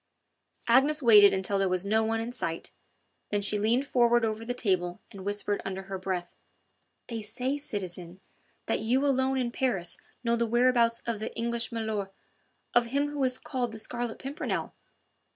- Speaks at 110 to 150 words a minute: No, average, 170 wpm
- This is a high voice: Yes, high, 225 Hz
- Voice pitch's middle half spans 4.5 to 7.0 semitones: No, average, 3.7 semitones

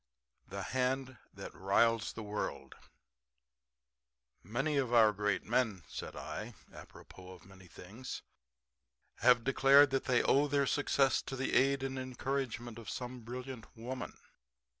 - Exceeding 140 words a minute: No, slow, 135 wpm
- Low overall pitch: Yes, low, 125 Hz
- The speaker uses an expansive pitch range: No, average, 3.6 semitones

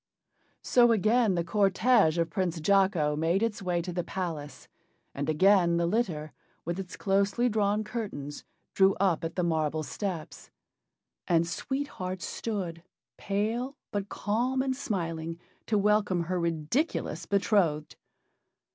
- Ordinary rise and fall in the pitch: Yes, average, 4.1 semitones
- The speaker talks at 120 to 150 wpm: Yes, slow, 135 wpm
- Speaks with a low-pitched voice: No, high, 190 Hz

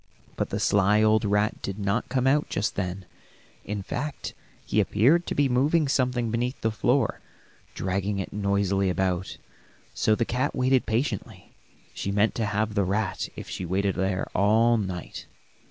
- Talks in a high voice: No, low, 105 Hz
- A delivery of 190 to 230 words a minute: No, average, 165 wpm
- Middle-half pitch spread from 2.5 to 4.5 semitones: Yes, average, 4.0 semitones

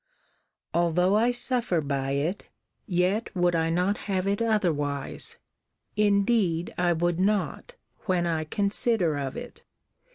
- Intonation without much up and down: No, average, 4.1 semitones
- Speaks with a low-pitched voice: No, medium, 180 Hz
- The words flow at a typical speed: No, slow, 125 wpm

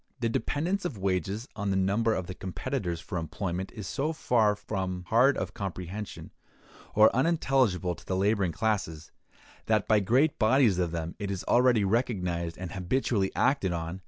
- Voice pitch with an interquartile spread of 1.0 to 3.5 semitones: No, average, 4.6 semitones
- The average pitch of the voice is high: No, low, 100 Hz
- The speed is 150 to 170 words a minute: Yes, average, 165 wpm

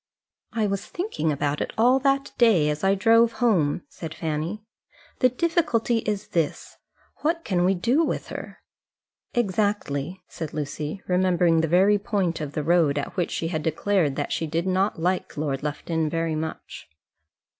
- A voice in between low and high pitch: Yes, medium, 180 Hz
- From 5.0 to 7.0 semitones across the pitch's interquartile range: Yes, wide, 5.6 semitones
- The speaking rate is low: No, average, 160 wpm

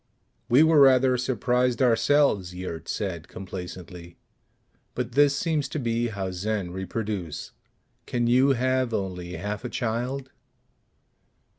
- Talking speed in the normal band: No, slow, 125 wpm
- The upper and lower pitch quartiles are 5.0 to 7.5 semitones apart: Yes, wide, 5.4 semitones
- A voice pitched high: No, low, 115 Hz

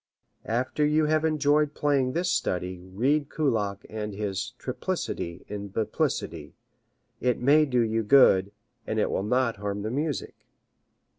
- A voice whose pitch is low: Yes, low, 120 Hz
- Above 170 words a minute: No, average, 140 wpm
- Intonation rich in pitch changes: Yes, wide, 6.2 semitones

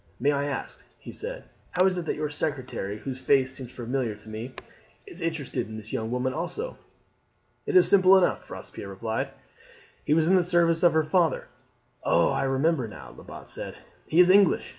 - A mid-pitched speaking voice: Yes, medium, 145 Hz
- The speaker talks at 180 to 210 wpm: Yes, average, 190 wpm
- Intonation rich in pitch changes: Yes, wide, 5.9 semitones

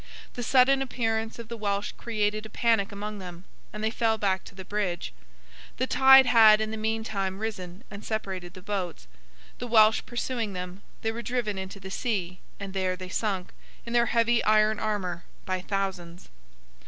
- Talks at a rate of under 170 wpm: No, average, 180 wpm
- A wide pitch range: No, average, 3.0 semitones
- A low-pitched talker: No, high, 210 Hz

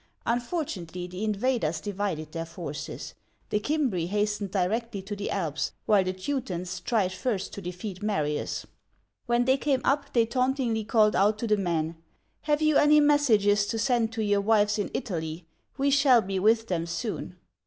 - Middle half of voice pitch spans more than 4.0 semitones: Yes, average, 4.7 semitones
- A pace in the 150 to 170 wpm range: Yes, average, 165 wpm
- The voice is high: Yes, high, 210 Hz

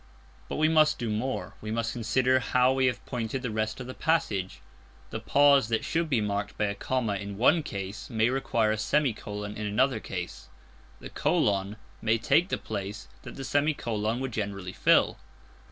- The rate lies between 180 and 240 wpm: Yes, average, 185 wpm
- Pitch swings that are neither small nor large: Yes, average, 4.2 semitones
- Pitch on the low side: Yes, low, 115 Hz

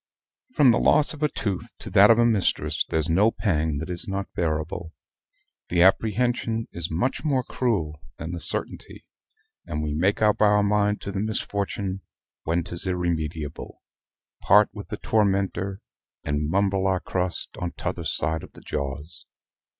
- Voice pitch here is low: Yes, very low, 95 Hz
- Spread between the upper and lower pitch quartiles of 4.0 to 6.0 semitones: Yes, average, 4.5 semitones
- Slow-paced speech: No, average, 160 wpm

